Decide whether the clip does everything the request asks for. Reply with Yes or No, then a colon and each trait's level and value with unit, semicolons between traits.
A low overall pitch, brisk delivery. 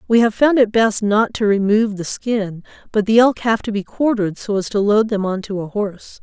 No: high, 210 Hz; fast, 250 wpm